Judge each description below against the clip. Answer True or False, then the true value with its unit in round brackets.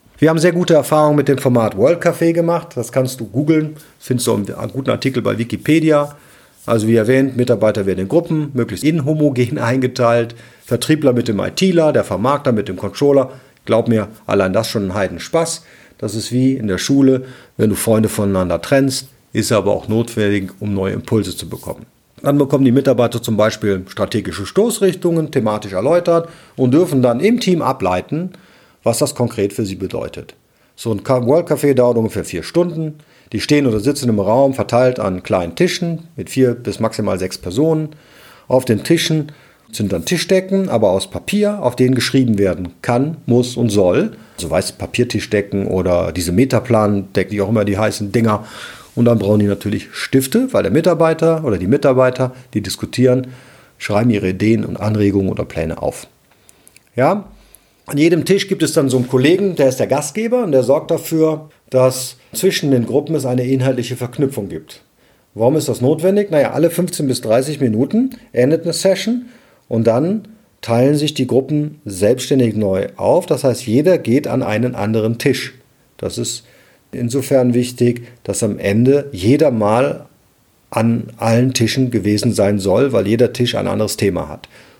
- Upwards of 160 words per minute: True (175 wpm)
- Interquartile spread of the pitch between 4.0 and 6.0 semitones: True (5.5 semitones)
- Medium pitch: False (125 Hz)